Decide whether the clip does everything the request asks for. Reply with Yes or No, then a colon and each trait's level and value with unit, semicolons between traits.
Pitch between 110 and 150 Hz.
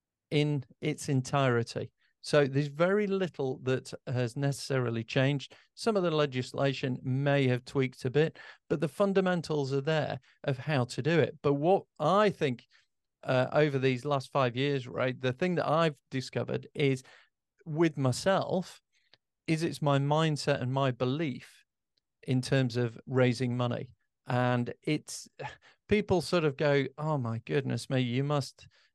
Yes: medium, 140 Hz